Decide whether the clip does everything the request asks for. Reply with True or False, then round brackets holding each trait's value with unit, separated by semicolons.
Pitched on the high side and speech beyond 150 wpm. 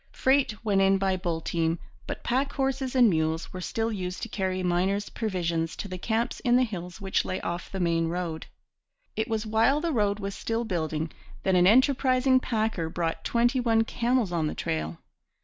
True (195 Hz; 190 wpm)